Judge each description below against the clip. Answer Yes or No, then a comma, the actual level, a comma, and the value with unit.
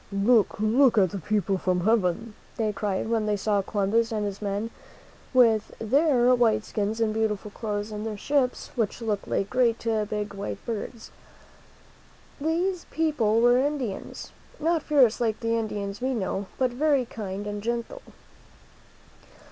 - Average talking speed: Yes, average, 150 wpm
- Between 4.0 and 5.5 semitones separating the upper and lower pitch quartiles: No, average, 3.0 semitones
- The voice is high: Yes, high, 220 Hz